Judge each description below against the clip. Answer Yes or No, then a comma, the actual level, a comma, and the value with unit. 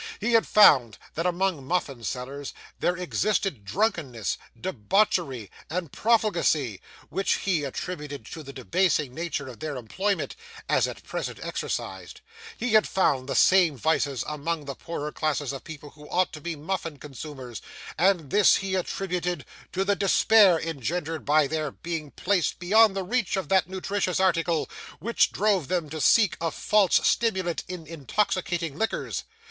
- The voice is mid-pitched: Yes, medium, 165 Hz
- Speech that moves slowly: No, average, 155 wpm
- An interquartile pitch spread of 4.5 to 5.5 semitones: Yes, average, 4.8 semitones